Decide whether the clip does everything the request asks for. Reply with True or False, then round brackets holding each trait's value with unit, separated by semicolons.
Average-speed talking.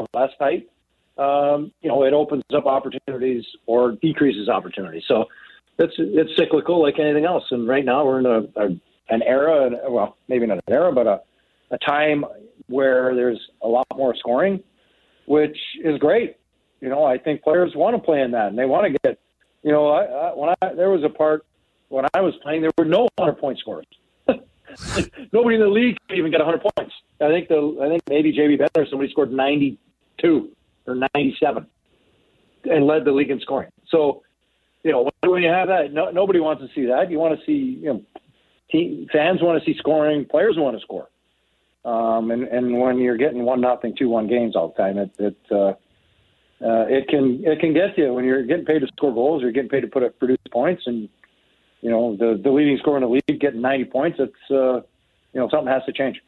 False (210 wpm)